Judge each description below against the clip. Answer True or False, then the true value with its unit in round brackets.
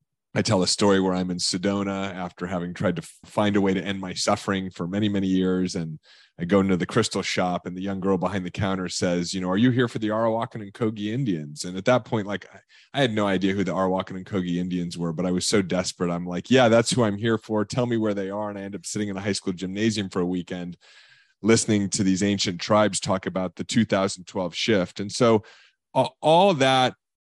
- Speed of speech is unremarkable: False (250 wpm)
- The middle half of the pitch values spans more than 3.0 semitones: False (2.7 semitones)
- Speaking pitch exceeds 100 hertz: False (95 Hz)